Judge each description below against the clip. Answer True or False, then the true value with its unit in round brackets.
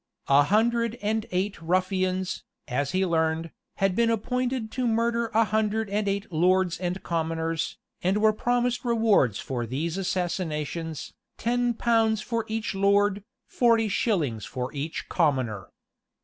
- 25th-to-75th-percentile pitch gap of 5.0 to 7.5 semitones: True (5.4 semitones)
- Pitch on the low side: False (195 Hz)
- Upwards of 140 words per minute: False (135 wpm)